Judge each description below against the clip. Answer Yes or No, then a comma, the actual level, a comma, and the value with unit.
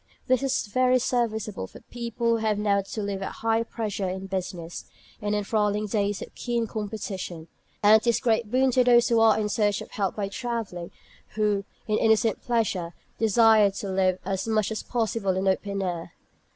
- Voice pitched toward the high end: Yes, high, 210 Hz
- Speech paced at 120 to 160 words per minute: No, average, 200 wpm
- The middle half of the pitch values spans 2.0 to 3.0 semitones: Yes, average, 2.7 semitones